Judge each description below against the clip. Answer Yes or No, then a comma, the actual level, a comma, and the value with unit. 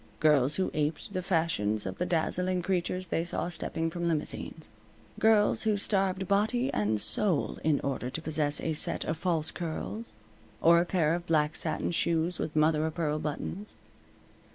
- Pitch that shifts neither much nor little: Yes, average, 3.2 semitones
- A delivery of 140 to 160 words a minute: No, average, 170 wpm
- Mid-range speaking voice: Yes, medium, 165 Hz